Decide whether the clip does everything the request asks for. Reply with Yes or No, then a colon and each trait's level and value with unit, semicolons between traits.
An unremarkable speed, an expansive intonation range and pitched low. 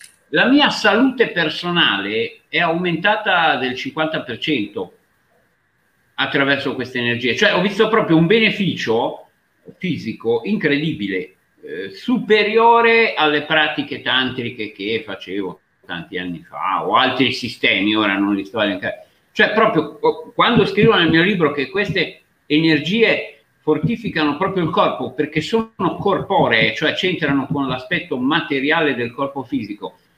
No: average, 125 wpm; wide, 7.6 semitones; medium, 160 Hz